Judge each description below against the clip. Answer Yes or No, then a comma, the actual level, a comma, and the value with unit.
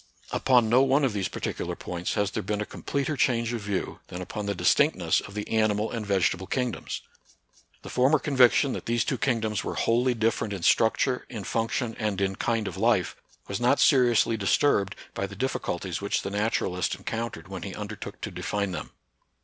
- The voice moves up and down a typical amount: Yes, average, 3.4 semitones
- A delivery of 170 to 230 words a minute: Yes, average, 190 wpm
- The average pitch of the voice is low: Yes, low, 110 Hz